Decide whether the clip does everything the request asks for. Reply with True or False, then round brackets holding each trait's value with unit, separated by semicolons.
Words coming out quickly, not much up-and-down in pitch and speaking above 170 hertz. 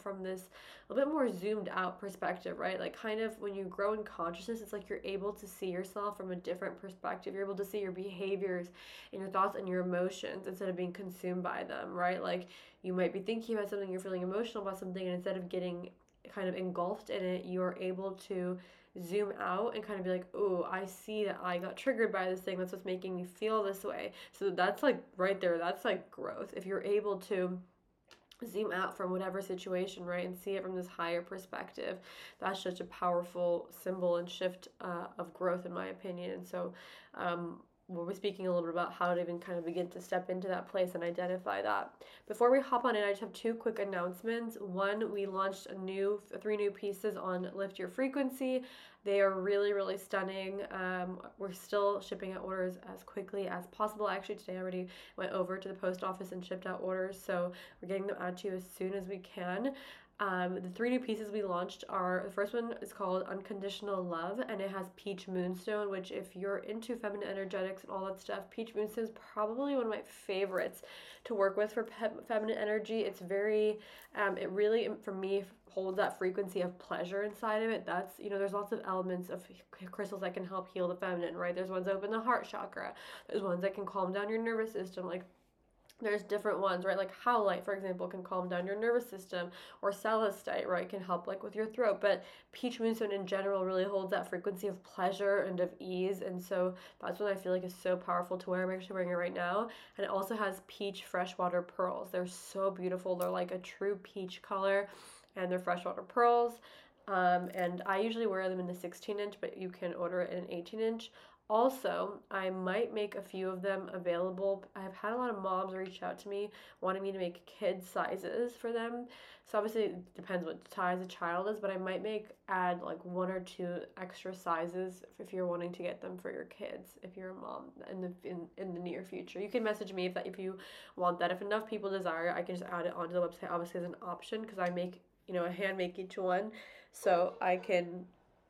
True (225 wpm; 2.0 semitones; 190 Hz)